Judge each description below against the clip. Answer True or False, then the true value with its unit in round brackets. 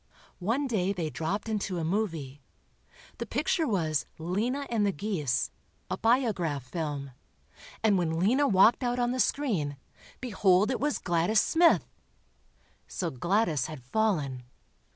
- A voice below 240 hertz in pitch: True (190 Hz)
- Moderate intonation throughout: False (6.4 semitones)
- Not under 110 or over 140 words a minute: True (135 wpm)